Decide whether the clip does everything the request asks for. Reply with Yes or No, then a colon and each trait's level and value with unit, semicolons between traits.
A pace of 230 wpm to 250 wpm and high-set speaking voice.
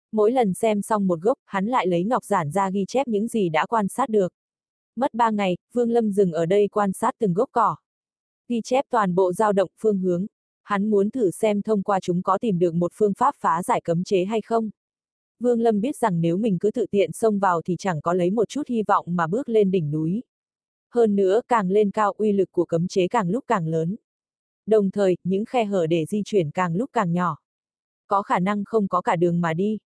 Yes: average, 240 wpm; high, 200 Hz